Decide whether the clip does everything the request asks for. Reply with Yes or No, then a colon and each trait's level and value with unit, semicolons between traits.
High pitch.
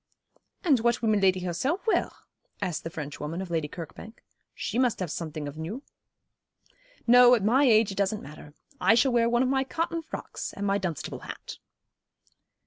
Yes: high, 210 Hz